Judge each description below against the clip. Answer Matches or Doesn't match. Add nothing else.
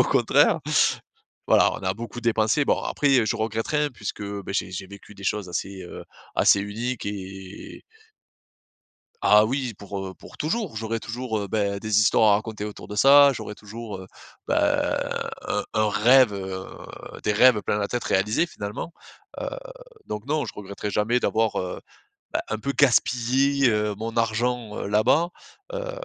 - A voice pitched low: Matches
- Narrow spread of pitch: Doesn't match